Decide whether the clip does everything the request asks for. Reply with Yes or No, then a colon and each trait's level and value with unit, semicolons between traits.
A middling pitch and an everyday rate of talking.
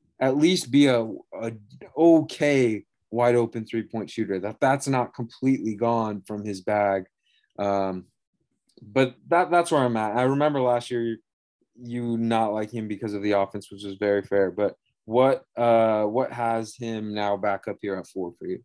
No: low, 115 Hz; average, 185 wpm